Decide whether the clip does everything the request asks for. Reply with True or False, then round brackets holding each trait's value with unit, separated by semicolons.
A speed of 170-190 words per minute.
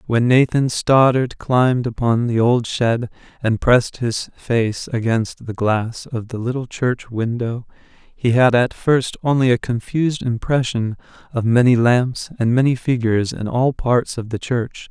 False (160 wpm)